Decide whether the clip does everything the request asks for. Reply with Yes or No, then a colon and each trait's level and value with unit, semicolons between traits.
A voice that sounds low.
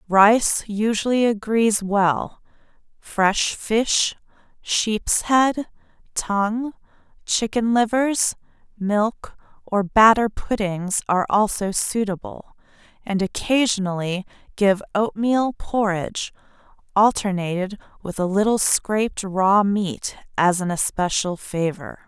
No: high, 205 Hz